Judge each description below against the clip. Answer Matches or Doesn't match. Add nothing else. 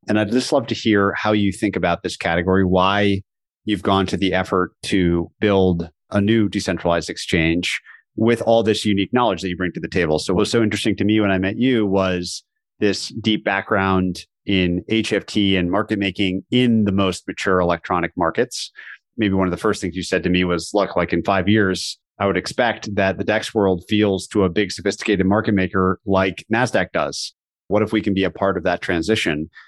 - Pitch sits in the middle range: Doesn't match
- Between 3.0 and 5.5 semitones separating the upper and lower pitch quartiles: Doesn't match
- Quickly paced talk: Matches